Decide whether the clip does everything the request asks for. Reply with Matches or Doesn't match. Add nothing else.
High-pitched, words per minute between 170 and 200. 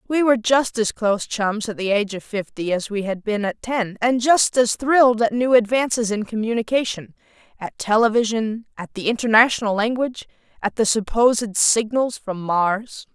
Matches